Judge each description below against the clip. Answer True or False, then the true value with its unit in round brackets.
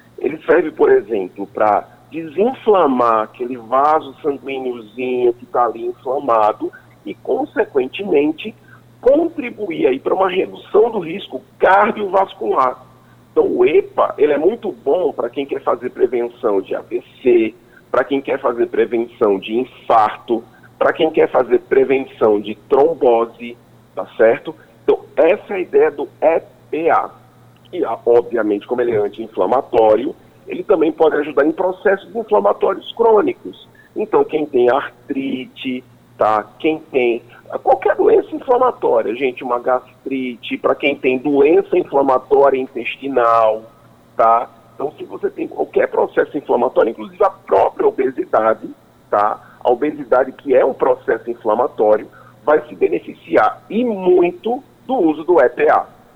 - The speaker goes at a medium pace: True (130 wpm)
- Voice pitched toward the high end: True (240 Hz)